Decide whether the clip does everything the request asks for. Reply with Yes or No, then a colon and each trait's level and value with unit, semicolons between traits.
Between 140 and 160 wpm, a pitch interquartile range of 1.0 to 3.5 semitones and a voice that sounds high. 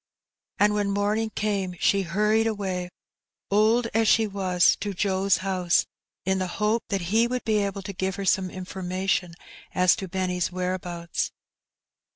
Yes: average, 155 wpm; narrow, 2.4 semitones; high, 195 Hz